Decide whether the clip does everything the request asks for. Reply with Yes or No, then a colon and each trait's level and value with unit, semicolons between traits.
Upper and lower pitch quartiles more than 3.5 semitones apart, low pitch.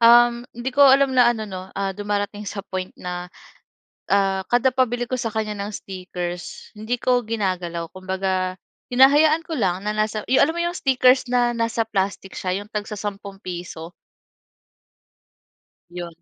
No: average, 4.5 semitones; high, 210 Hz